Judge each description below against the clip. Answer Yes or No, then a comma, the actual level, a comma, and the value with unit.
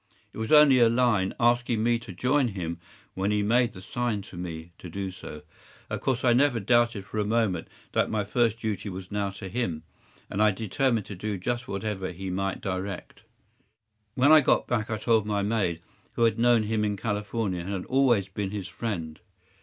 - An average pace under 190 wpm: No, average, 200 wpm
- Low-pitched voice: Yes, low, 105 Hz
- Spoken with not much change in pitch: No, average, 3.8 semitones